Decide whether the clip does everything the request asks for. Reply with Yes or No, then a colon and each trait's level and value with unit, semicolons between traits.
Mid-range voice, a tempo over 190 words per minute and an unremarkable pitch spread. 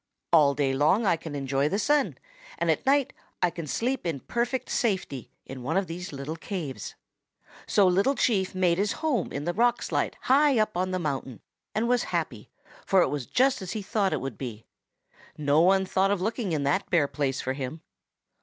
No: medium, 180 Hz; average, 200 wpm; wide, 7.0 semitones